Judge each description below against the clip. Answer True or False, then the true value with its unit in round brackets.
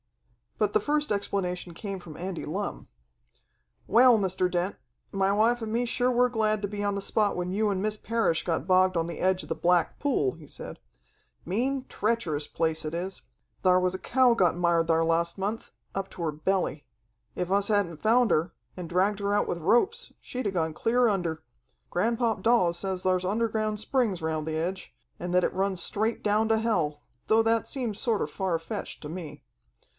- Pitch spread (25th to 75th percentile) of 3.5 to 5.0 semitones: True (4.3 semitones)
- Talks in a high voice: True (195 Hz)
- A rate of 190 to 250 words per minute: True (195 wpm)